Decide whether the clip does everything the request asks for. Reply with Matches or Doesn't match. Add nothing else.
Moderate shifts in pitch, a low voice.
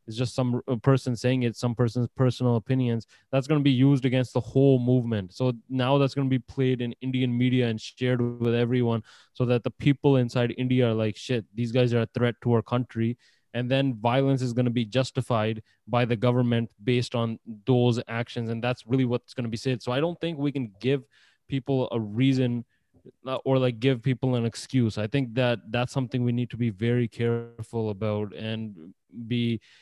Doesn't match